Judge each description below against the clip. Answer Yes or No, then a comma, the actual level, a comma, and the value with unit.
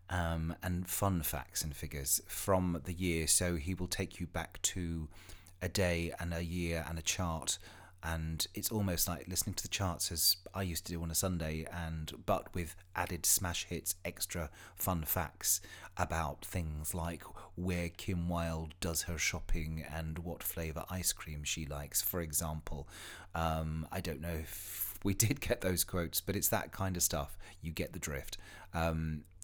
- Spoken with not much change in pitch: Yes, narrow, 2.1 semitones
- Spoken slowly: No, average, 180 wpm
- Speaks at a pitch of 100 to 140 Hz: No, very low, 85 Hz